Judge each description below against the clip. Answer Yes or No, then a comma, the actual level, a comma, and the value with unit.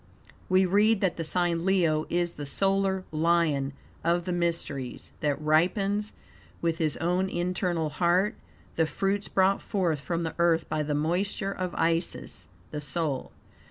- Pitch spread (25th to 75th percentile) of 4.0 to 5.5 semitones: No, average, 3.2 semitones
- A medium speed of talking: Yes, average, 150 wpm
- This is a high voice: No, medium, 170 Hz